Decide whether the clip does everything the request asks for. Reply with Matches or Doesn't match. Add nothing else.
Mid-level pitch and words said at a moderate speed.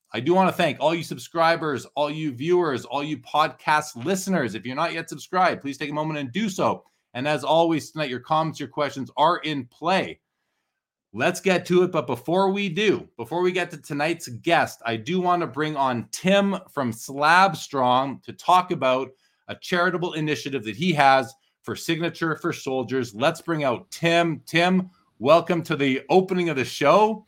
Matches